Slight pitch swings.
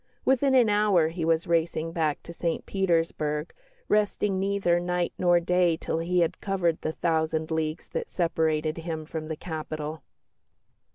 Yes: narrow, 2.1 semitones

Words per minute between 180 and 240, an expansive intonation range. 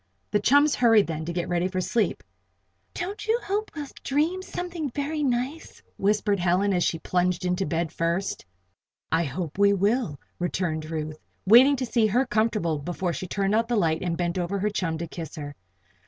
Yes: average, 185 wpm; wide, 6.1 semitones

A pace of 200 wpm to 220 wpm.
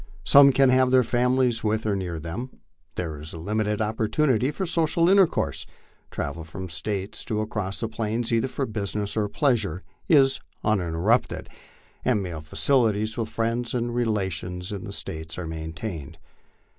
No: average, 160 wpm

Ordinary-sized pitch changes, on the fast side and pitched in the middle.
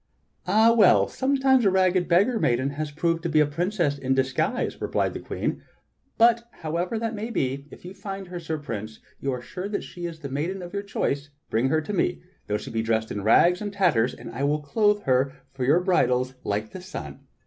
No: wide, 6.7 semitones; fast, 225 wpm; medium, 165 Hz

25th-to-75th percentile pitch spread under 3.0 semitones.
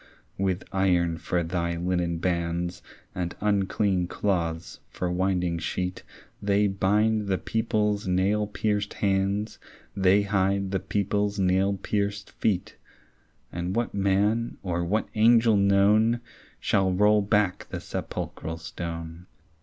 Yes: narrow, 2.6 semitones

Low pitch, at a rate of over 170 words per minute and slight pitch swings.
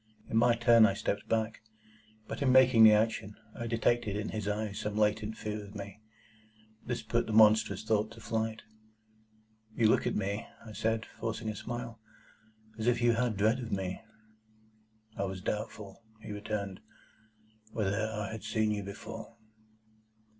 No: low, 110 Hz; average, 165 wpm; narrow, 1.7 semitones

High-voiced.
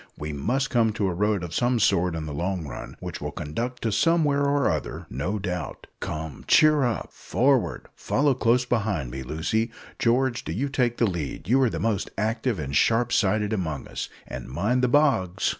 No: low, 110 Hz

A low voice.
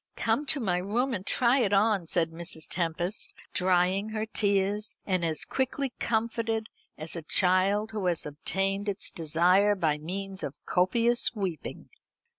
No: high, 195 Hz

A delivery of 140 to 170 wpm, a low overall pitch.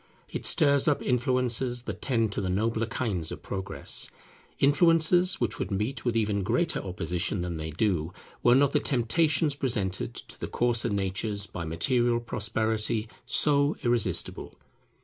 Yes: average, 150 wpm; low, 115 Hz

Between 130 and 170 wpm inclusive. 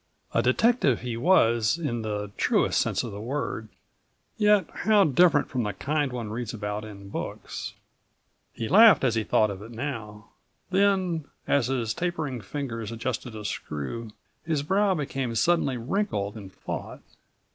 Yes: average, 155 wpm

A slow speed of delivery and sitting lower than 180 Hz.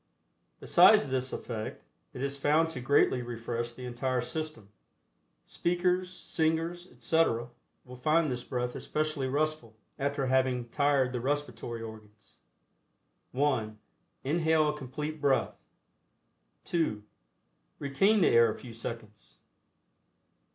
Yes: slow, 115 wpm; low, 135 Hz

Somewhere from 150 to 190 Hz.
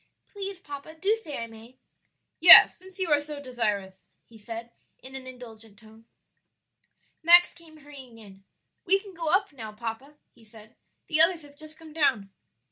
No: very high, 275 Hz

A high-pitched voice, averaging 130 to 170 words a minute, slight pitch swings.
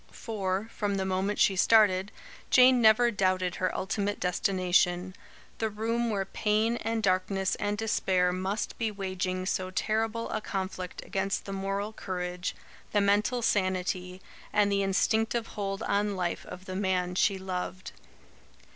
Yes: high, 195 Hz; average, 145 wpm; narrow, 2.3 semitones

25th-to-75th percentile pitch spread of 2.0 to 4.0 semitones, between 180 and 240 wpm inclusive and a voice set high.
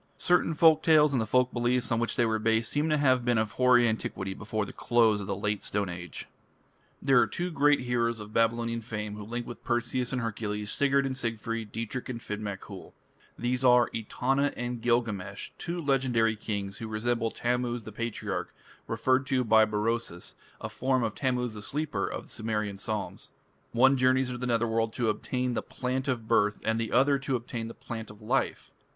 No: average, 2.7 semitones; average, 200 wpm; low, 115 Hz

